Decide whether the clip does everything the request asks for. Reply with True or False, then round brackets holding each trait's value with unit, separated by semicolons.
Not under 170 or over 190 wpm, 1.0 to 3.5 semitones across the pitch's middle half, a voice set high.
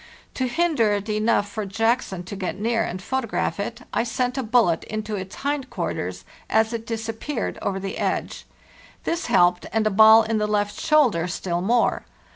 True (180 wpm; 2.9 semitones; 220 Hz)